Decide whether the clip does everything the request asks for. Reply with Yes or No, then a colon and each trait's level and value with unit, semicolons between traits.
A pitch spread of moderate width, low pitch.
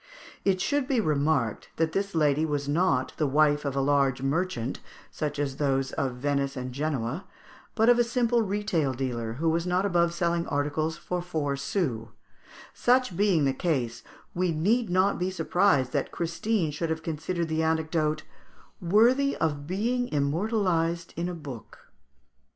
No: average, 4.7 semitones; medium, 160 Hz